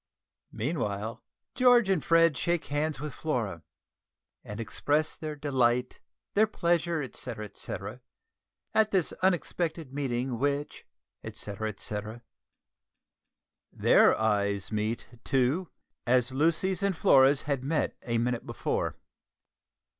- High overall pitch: No, medium, 140 Hz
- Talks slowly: Yes, slow, 105 wpm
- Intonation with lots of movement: Yes, wide, 6.0 semitones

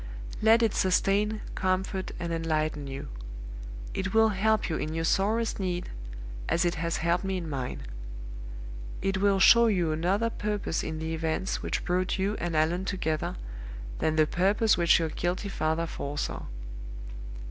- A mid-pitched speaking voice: Yes, medium, 180 Hz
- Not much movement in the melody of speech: No, average, 3.7 semitones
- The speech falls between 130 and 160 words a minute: Yes, average, 155 wpm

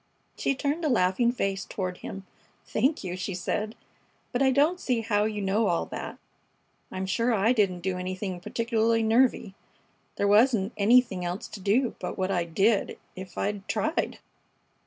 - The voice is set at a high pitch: Yes, high, 210 Hz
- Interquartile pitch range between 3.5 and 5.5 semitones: Yes, average, 4.1 semitones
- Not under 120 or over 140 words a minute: No, average, 165 wpm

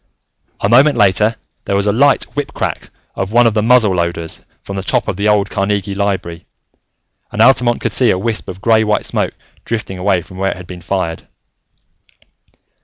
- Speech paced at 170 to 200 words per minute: Yes, average, 185 wpm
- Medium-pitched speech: No, low, 100 Hz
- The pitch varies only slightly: No, average, 3.3 semitones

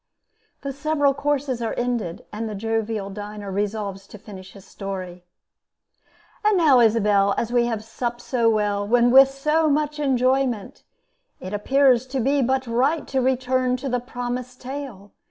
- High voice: Yes, high, 245 Hz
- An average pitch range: Yes, average, 4.3 semitones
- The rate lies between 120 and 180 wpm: Yes, average, 155 wpm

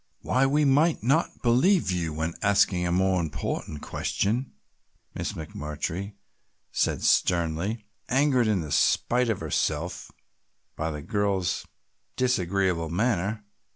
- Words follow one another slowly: Yes, slow, 115 wpm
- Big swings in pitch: Yes, wide, 6.4 semitones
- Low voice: Yes, low, 100 Hz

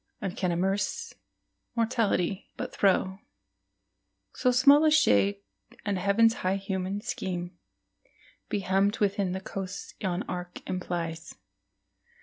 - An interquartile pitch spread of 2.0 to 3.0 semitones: Yes, narrow, 2.4 semitones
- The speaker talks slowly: Yes, slow, 115 wpm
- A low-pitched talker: No, high, 190 Hz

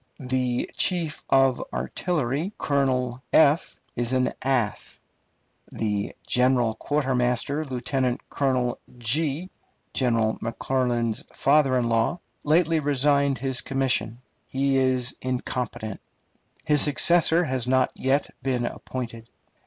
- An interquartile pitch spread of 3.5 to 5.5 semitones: No, narrow, 2.6 semitones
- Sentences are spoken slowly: Yes, slow, 100 wpm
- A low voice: Yes, low, 130 Hz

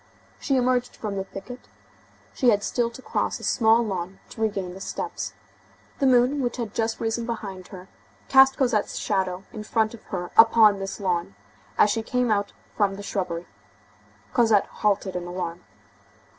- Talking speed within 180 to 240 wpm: No, average, 170 wpm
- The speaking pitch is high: Yes, high, 210 Hz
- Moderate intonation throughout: Yes, average, 3.6 semitones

